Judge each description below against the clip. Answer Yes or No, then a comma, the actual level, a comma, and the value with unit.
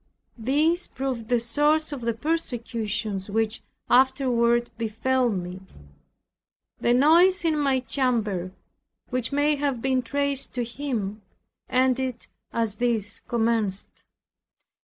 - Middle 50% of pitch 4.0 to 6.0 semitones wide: No, average, 3.5 semitones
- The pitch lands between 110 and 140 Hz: No, high, 245 Hz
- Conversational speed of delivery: No, slow, 110 wpm